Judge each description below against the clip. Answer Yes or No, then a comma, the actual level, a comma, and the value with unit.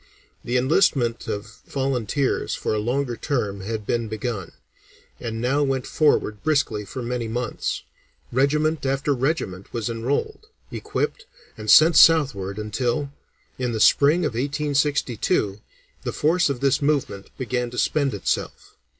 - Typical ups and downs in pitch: Yes, average, 4.1 semitones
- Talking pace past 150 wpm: No, slow, 135 wpm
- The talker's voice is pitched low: Yes, low, 125 Hz